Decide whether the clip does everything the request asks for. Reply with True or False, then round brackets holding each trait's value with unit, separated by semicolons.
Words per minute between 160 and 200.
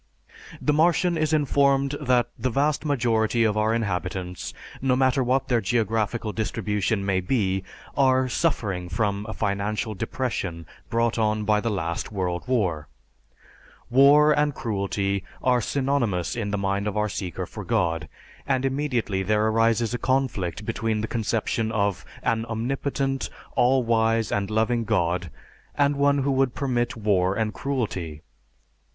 False (145 wpm)